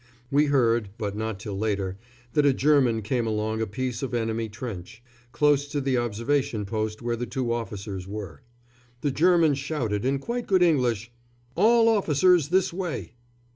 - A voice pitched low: Yes, low, 120 Hz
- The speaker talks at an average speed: Yes, average, 165 wpm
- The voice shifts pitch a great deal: No, average, 5.0 semitones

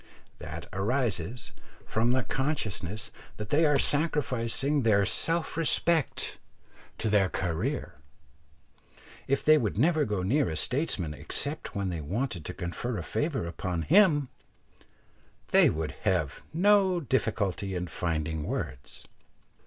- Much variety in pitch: Yes, wide, 8.4 semitones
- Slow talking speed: Yes, slow, 125 wpm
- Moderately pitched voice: No, low, 110 Hz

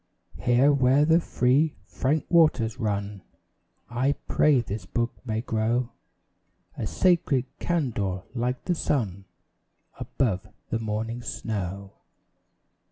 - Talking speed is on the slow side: Yes, slow, 105 wpm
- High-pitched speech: No, low, 120 Hz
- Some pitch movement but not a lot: Yes, average, 4.5 semitones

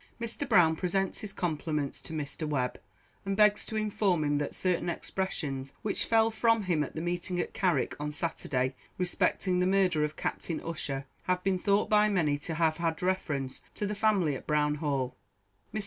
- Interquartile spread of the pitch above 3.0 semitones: Yes, average, 4.6 semitones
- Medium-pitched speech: Yes, medium, 175 Hz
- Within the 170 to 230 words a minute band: Yes, average, 185 wpm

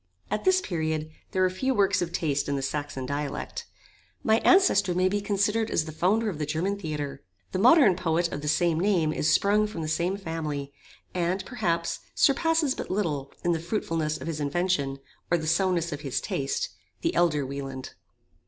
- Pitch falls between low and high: Yes, medium, 170 Hz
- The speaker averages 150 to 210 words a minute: Yes, average, 190 wpm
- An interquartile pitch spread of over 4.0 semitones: Yes, average, 5.0 semitones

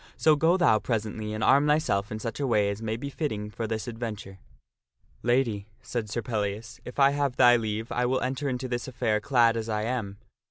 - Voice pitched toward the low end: Yes, low, 115 Hz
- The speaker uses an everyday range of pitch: Yes, average, 3.3 semitones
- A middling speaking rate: No, fast, 225 wpm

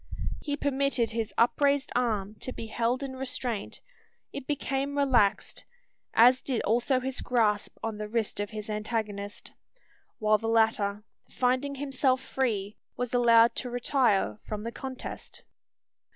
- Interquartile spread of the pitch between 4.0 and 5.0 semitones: No, average, 3.6 semitones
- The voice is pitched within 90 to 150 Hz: No, high, 240 Hz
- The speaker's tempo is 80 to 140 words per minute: Yes, slow, 135 wpm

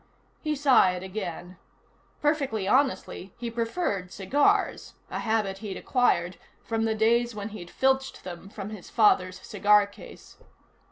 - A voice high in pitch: Yes, high, 215 Hz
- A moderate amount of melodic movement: Yes, average, 4.1 semitones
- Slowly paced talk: Yes, slow, 130 wpm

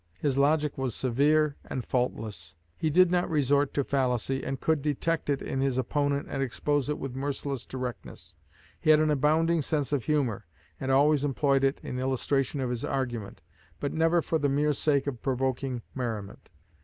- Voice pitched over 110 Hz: Yes, medium, 140 Hz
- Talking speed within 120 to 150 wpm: No, average, 180 wpm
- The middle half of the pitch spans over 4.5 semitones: No, narrow, 2.5 semitones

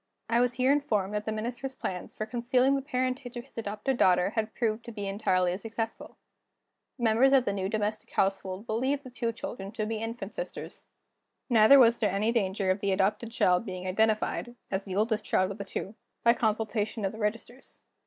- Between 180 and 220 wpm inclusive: Yes, average, 200 wpm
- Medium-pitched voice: No, high, 220 Hz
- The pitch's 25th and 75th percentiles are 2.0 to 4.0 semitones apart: Yes, average, 3.2 semitones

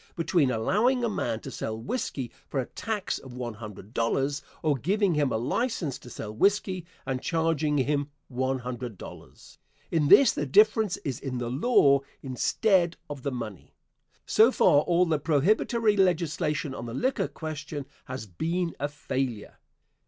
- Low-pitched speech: No, medium, 145 Hz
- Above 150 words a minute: Yes, average, 165 wpm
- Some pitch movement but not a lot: No, wide, 6.1 semitones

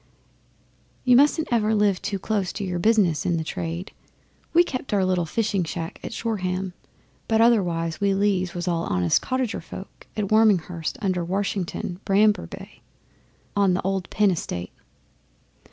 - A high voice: Yes, high, 195 Hz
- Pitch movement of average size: Yes, average, 3.5 semitones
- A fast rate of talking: No, average, 155 wpm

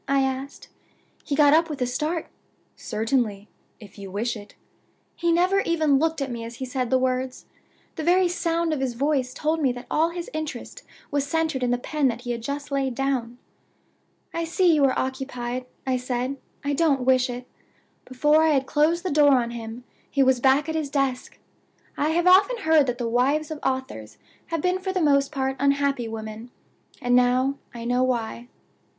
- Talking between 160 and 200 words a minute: Yes, average, 195 wpm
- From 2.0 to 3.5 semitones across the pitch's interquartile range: No, average, 3.9 semitones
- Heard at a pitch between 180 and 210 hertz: No, very high, 270 Hz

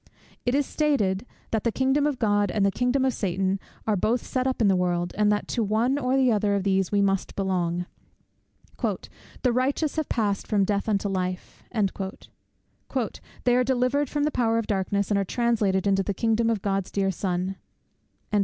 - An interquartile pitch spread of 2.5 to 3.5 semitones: No, average, 4.3 semitones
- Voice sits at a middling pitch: No, high, 210 Hz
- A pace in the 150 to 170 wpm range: No, average, 190 wpm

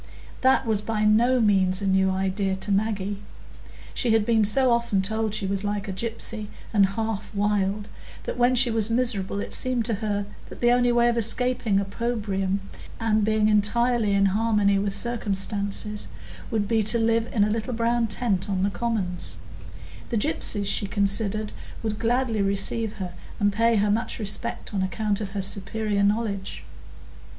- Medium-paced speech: Yes, average, 170 wpm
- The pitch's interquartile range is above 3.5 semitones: No, narrow, 2.4 semitones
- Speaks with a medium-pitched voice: No, high, 210 Hz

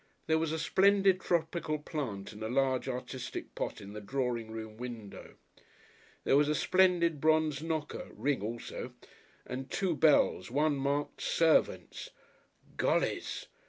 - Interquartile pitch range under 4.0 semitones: No, average, 4.6 semitones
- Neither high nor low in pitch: Yes, medium, 145 Hz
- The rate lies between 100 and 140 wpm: Yes, slow, 135 wpm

